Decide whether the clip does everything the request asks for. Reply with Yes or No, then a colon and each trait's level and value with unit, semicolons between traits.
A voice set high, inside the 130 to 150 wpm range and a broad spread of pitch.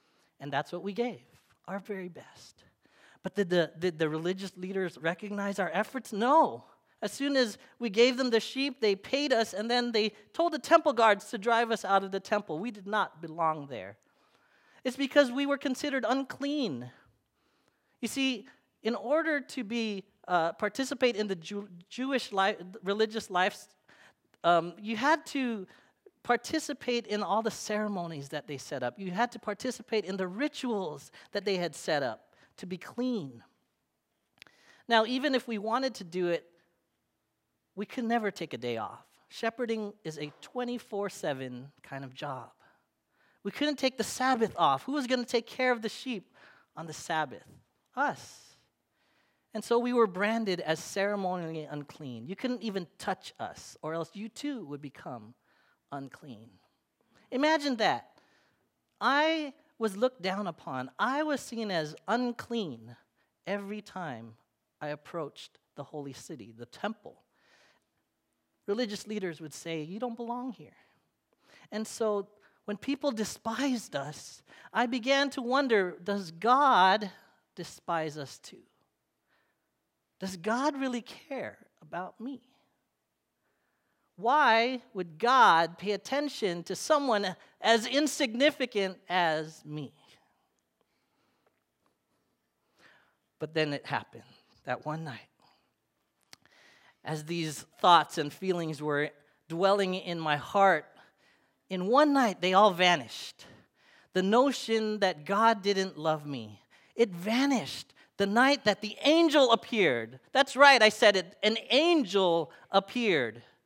Yes: high, 205 Hz; average, 140 wpm; wide, 6.5 semitones